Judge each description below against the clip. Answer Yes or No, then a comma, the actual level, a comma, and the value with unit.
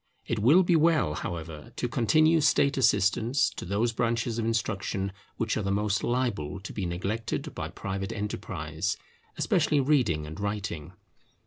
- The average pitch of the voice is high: No, low, 105 Hz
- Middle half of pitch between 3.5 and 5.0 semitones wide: Yes, average, 4.3 semitones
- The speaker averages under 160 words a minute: Yes, average, 150 wpm